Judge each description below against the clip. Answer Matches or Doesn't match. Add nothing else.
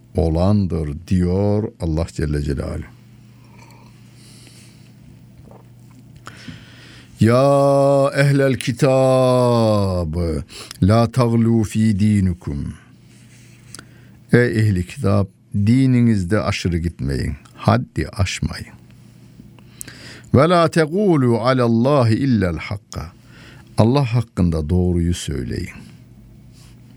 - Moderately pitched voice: Doesn't match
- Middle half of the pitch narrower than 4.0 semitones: Doesn't match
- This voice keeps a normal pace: Doesn't match